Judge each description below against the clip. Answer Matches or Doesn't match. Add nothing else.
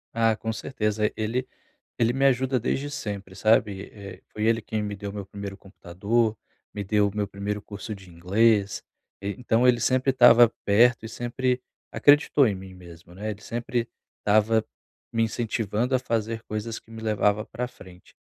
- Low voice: Matches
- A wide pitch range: Doesn't match